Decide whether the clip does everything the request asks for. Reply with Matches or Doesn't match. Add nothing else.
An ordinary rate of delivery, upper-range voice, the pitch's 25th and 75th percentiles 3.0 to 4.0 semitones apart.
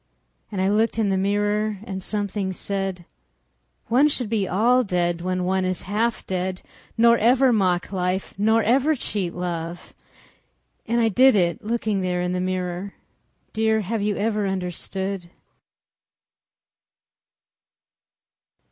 Doesn't match